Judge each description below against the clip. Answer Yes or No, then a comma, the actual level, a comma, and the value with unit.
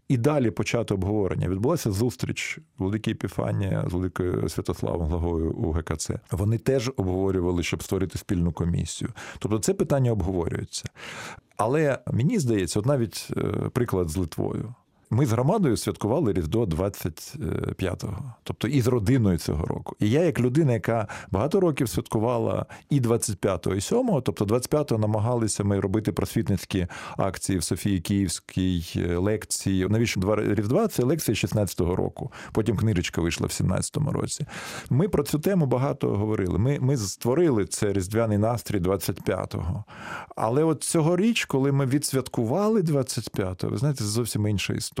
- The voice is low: Yes, low, 110 Hz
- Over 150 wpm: No, average, 145 wpm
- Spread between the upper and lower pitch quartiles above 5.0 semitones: Yes, wide, 5.5 semitones